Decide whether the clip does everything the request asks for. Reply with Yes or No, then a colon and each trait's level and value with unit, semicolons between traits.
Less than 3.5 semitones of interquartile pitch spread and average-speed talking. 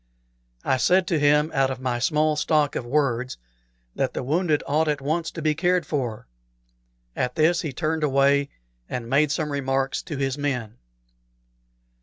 Yes: average, 2.7 semitones; average, 165 wpm